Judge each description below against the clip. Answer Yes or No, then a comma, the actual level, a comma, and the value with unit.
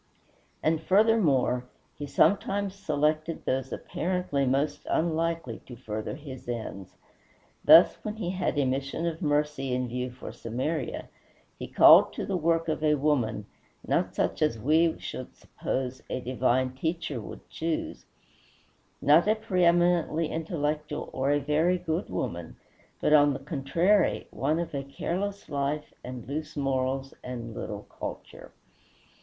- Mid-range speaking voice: Yes, medium, 150 Hz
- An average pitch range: Yes, average, 4.3 semitones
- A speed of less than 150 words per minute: Yes, average, 140 wpm